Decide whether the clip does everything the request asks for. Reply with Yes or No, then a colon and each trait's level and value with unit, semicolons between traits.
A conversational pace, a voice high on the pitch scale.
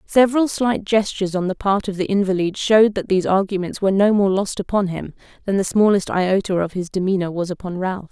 No: fast, 215 wpm; high, 195 Hz